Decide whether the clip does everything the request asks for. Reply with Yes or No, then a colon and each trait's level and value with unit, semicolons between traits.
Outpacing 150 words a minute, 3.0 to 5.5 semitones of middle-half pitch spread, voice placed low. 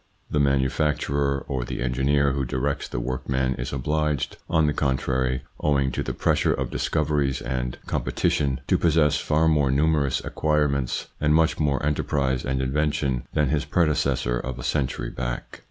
No: average, 160 wpm; narrow, 2.5 semitones; very low, 70 Hz